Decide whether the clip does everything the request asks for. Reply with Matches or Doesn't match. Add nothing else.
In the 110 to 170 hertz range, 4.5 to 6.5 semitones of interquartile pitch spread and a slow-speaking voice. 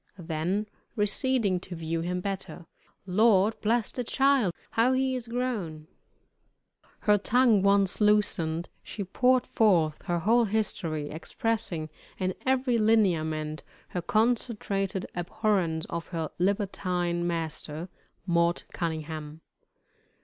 Doesn't match